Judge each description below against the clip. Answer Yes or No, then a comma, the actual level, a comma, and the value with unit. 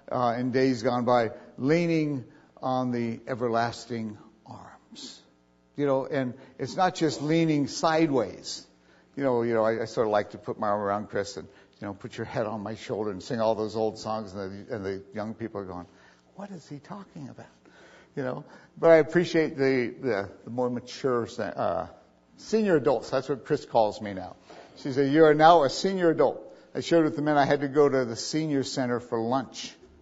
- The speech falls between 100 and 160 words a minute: No, fast, 205 wpm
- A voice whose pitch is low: Yes, low, 125 Hz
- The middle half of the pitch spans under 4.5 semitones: No, average, 5.1 semitones